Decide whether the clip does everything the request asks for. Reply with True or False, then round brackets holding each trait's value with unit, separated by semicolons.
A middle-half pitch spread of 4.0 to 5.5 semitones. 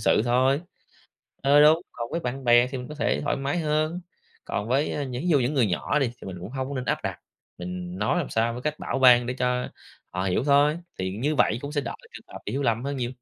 False (3.5 semitones)